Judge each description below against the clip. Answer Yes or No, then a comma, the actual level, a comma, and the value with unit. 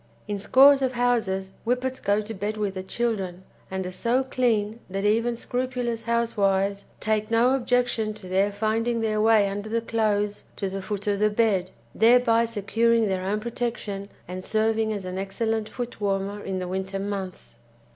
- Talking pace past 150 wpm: Yes, average, 170 wpm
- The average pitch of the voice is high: Yes, high, 215 Hz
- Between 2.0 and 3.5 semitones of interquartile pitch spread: Yes, average, 2.9 semitones